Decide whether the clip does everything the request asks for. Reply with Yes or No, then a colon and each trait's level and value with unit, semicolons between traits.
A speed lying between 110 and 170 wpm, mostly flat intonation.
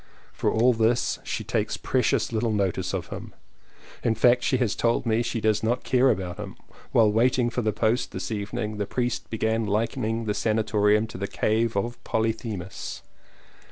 No: average, 180 wpm; narrow, 2.1 semitones